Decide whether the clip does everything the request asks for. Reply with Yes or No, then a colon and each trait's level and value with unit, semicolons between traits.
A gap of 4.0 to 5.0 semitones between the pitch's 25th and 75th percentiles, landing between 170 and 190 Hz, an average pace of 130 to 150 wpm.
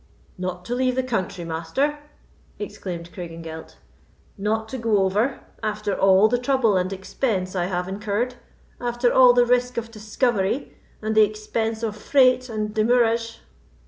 No: average, 4.3 semitones; high, 215 Hz; average, 145 wpm